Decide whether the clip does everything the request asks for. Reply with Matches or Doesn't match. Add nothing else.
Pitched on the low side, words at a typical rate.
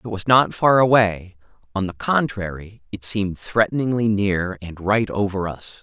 Matches